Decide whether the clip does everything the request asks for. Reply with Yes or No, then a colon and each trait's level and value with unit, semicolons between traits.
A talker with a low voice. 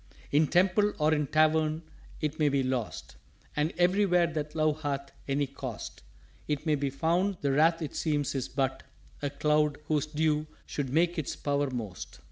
No: medium, 150 Hz